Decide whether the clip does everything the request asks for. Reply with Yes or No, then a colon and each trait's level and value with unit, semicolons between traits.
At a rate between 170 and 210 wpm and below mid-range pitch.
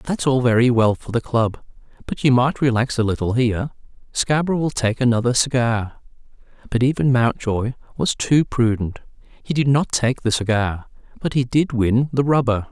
Yes: average, 175 wpm; low, 125 Hz